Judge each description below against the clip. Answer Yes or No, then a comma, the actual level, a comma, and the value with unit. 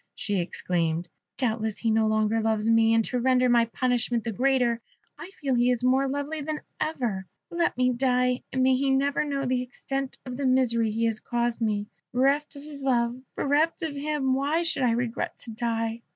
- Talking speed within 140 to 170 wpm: No, average, 195 wpm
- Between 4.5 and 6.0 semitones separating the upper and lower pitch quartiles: No, average, 3.2 semitones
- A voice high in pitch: Yes, very high, 250 Hz